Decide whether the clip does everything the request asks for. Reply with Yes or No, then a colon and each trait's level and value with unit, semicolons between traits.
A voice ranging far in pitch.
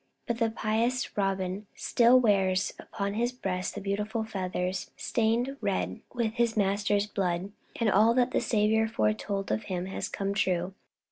No: average, 3.0 semitones